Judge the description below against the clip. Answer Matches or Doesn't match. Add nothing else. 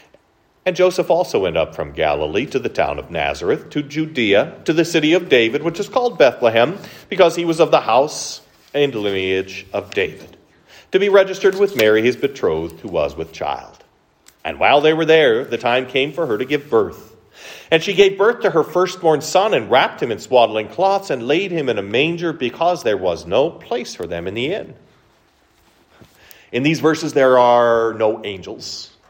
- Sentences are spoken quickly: Doesn't match